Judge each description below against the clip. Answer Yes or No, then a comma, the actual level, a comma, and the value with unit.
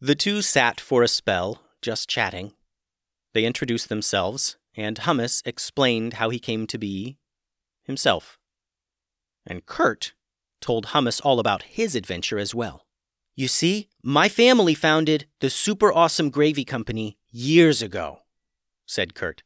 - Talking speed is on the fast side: No, slow, 135 wpm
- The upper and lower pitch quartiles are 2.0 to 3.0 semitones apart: No, wide, 5.4 semitones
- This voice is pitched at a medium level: No, low, 120 Hz